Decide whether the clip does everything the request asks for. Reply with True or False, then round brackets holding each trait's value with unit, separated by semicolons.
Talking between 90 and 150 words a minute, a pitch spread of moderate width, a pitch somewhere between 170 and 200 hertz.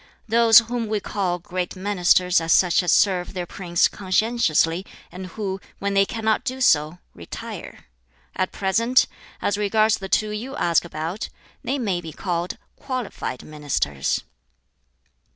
True (140 wpm; 3.9 semitones; 190 Hz)